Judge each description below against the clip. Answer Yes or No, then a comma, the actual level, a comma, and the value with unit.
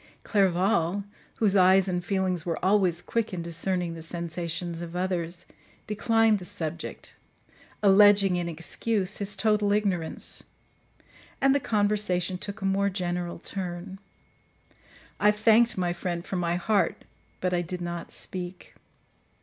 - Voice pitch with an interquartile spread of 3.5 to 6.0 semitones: No, average, 2.8 semitones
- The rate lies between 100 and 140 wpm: Yes, slow, 135 wpm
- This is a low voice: No, medium, 185 Hz